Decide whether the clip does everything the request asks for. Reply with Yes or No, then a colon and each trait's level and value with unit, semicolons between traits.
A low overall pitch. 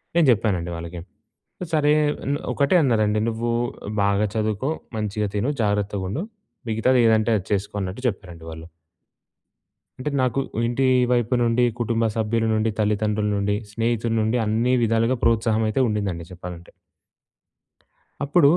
Yes: low, 110 Hz